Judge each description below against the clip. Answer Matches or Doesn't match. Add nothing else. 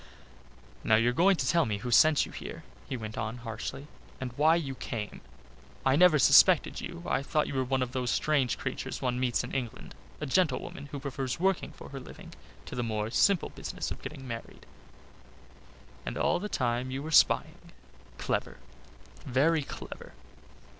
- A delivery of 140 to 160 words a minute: Doesn't match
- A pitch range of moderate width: Matches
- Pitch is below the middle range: Matches